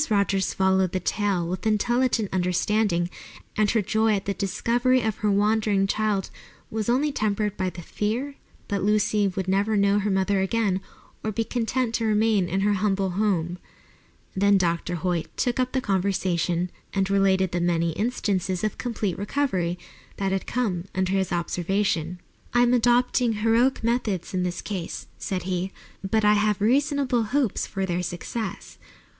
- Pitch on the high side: Yes, high, 200 Hz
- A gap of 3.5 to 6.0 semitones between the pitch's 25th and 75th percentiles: No, average, 3.0 semitones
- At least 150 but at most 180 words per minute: Yes, average, 160 wpm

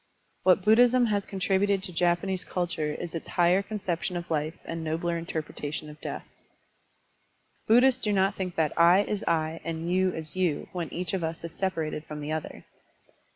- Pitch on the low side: No, medium, 175 Hz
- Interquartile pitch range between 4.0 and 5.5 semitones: No, average, 3.0 semitones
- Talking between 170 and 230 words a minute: Yes, average, 180 wpm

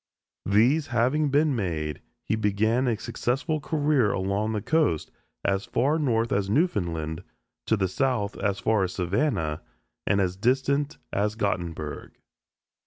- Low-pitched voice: Yes, low, 110 Hz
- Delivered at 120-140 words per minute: Yes, slow, 135 wpm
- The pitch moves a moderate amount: No, wide, 5.7 semitones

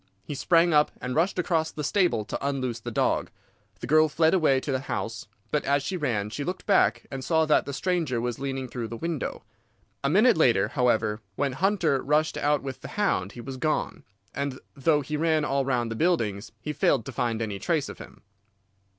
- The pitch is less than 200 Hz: Yes, medium, 140 Hz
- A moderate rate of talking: No, fast, 210 wpm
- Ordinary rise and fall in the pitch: Yes, average, 4.4 semitones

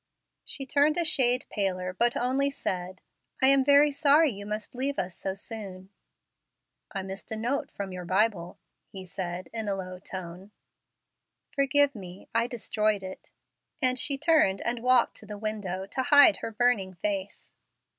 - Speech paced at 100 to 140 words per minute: No, average, 165 wpm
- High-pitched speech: Yes, high, 215 Hz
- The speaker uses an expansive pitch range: Yes, wide, 5.7 semitones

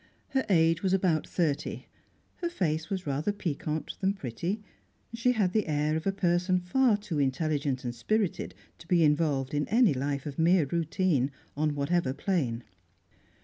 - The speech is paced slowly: No, average, 160 wpm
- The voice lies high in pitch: No, medium, 165 Hz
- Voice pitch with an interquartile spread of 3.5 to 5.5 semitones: Yes, average, 4.7 semitones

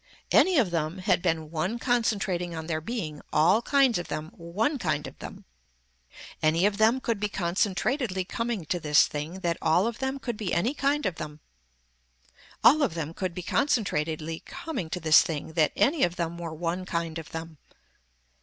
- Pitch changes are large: Yes, wide, 6.0 semitones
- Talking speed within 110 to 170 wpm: No, average, 185 wpm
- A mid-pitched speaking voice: Yes, medium, 175 Hz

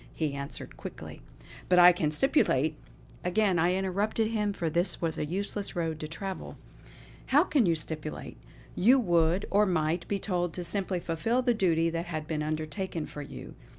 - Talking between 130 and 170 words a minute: No, average, 180 wpm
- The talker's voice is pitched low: No, medium, 175 Hz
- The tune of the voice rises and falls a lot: No, average, 4.0 semitones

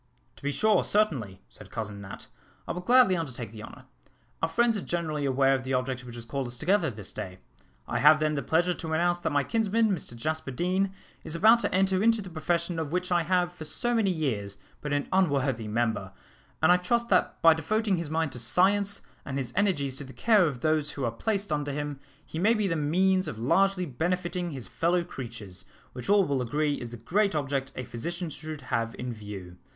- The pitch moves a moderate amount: No, wide, 6.3 semitones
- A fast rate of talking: Yes, fast, 220 wpm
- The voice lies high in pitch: No, medium, 155 Hz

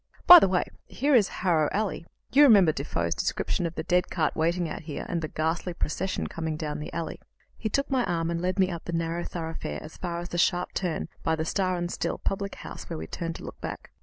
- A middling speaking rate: No, fast, 240 wpm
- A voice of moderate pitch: Yes, medium, 170 Hz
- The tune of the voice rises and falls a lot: No, narrow, 2.5 semitones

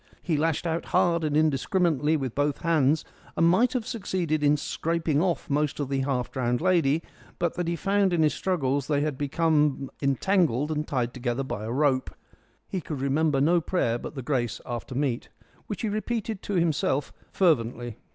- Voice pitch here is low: No, medium, 150 Hz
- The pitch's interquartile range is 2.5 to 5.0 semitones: Yes, average, 4.0 semitones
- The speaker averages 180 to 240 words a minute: Yes, average, 185 wpm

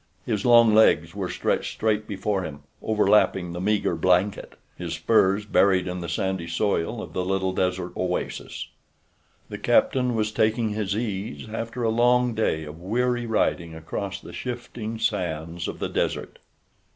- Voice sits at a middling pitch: No, low, 100 Hz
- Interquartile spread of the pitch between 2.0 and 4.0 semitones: Yes, average, 3.6 semitones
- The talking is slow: No, average, 155 wpm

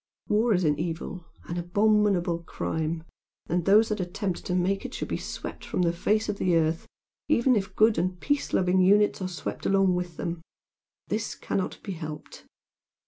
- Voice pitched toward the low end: No, medium, 185 Hz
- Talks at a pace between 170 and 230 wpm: Yes, average, 180 wpm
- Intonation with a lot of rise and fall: No, average, 3.3 semitones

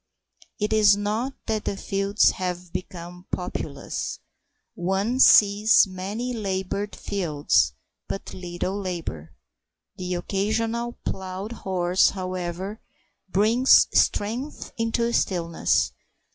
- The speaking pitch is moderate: No, high, 195 Hz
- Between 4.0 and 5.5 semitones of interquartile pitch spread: No, average, 3.1 semitones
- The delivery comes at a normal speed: No, slow, 100 wpm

